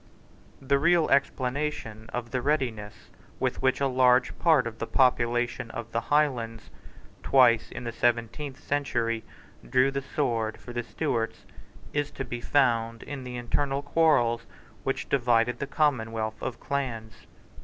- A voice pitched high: No, low, 125 Hz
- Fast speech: No, average, 145 wpm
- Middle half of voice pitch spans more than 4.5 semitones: No, average, 3.3 semitones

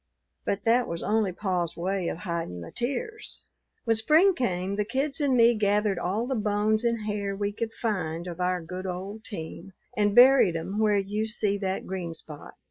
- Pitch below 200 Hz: No, high, 205 Hz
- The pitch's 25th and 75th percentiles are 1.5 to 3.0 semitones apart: No, average, 3.7 semitones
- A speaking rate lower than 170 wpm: No, average, 190 wpm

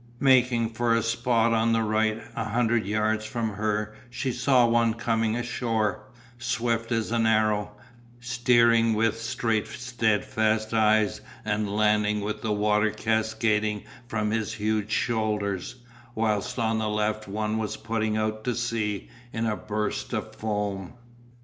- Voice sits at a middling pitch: No, low, 110 Hz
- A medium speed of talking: Yes, average, 145 wpm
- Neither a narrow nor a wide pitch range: No, narrow, 1.4 semitones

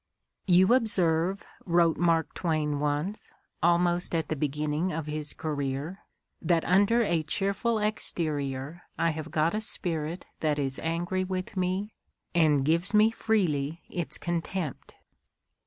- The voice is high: No, medium, 170 Hz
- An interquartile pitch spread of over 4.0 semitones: No, average, 3.5 semitones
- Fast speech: No, average, 150 wpm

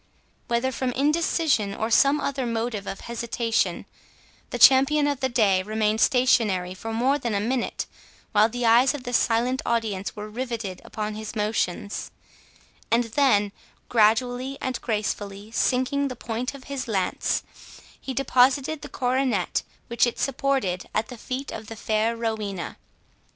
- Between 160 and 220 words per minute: No, average, 150 wpm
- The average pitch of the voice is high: Yes, high, 235 Hz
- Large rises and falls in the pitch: No, average, 3.3 semitones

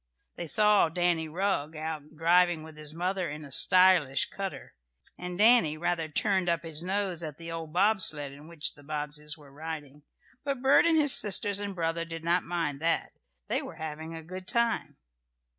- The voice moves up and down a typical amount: Yes, average, 3.4 semitones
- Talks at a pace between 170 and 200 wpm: Yes, average, 185 wpm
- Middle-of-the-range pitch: Yes, medium, 165 Hz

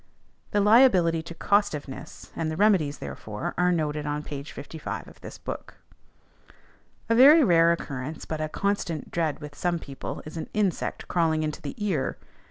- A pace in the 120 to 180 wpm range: Yes, average, 165 wpm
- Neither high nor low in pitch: Yes, medium, 165 Hz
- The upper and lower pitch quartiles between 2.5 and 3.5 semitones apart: No, average, 4.8 semitones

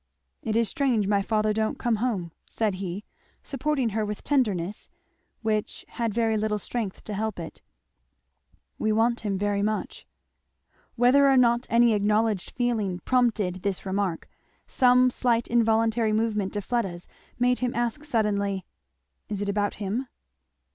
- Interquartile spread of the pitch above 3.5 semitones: No, average, 2.8 semitones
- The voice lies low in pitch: No, high, 220 Hz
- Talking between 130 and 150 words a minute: Yes, average, 145 wpm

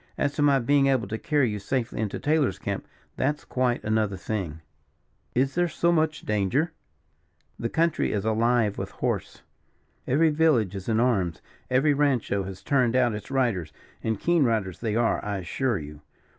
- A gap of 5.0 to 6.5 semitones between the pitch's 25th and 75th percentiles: Yes, average, 5.3 semitones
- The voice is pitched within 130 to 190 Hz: No, low, 120 Hz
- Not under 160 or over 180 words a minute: Yes, average, 170 wpm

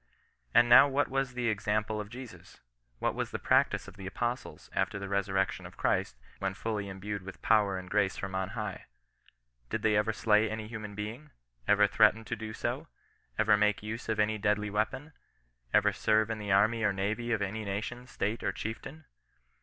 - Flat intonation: Yes, narrow, 2.0 semitones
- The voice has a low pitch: Yes, low, 105 Hz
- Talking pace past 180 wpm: Yes, average, 195 wpm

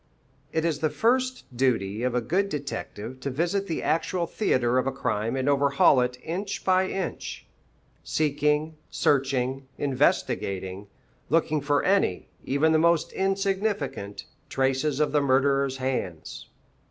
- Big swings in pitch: No, average, 4.3 semitones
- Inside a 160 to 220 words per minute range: No, slow, 135 wpm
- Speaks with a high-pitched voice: No, medium, 140 Hz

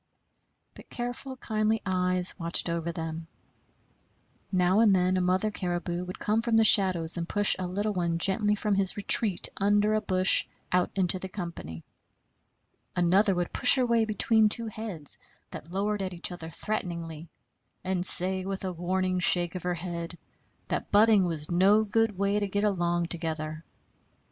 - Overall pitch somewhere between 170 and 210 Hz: Yes, medium, 185 Hz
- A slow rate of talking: No, average, 165 wpm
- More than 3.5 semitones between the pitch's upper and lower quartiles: No, average, 3.1 semitones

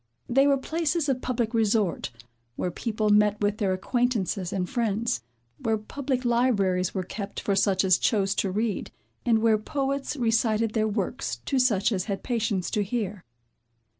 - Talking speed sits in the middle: Yes, average, 165 wpm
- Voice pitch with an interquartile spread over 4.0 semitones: No, average, 3.6 semitones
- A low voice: No, high, 220 Hz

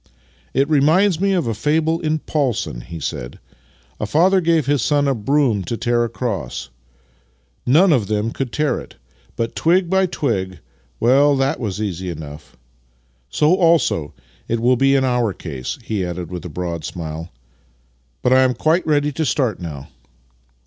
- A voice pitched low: Yes, low, 120 Hz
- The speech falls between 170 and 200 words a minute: Yes, average, 175 wpm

